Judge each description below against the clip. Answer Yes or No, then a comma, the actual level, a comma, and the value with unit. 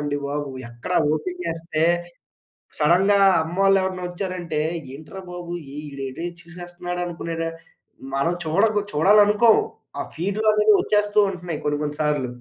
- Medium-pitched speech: Yes, medium, 175 Hz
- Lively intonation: No, average, 4.4 semitones